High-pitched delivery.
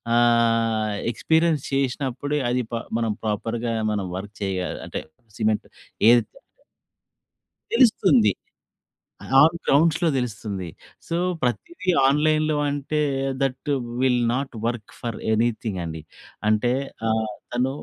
No: low, 120 Hz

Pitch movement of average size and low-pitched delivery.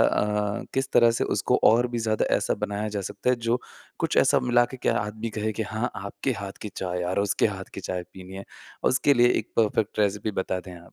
Yes: average, 3.0 semitones; low, 105 Hz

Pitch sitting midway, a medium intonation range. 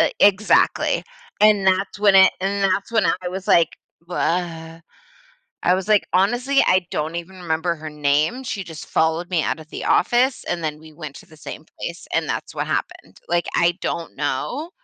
Yes: medium, 175 Hz; average, 3.6 semitones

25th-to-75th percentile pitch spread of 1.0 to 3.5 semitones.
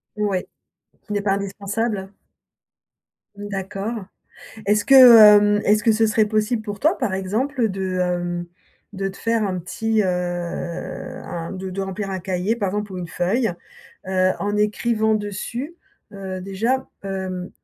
Yes: narrow, 2.6 semitones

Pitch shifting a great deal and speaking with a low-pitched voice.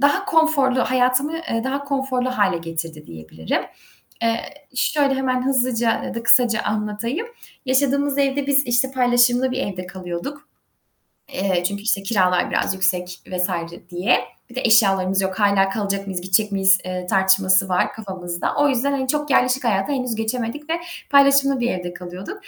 No: wide, 6.0 semitones; high, 230 Hz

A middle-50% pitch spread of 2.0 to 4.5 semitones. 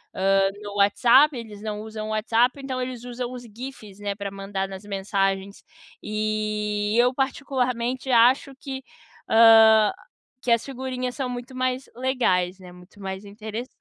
Yes: average, 3.7 semitones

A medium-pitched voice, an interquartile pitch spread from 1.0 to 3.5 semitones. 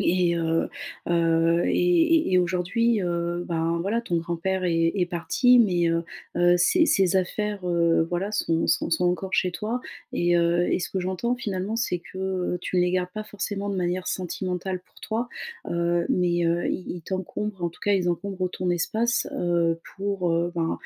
Yes: medium, 180 Hz; narrow, 2.5 semitones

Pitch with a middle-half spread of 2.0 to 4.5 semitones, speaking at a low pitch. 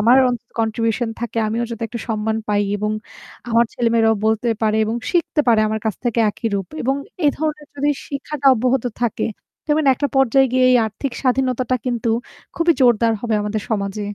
No: average, 2.9 semitones; high, 235 Hz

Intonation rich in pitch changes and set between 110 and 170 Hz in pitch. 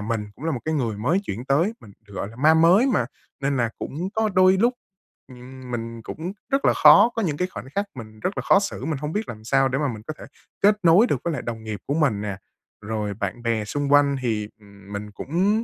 Yes: wide, 7.4 semitones; low, 135 Hz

